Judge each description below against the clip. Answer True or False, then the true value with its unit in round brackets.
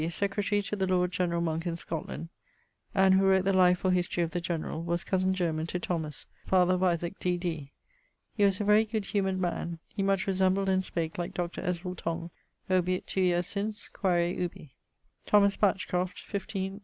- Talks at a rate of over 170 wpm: True (185 wpm)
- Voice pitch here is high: False (180 Hz)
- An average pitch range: False (2.0 semitones)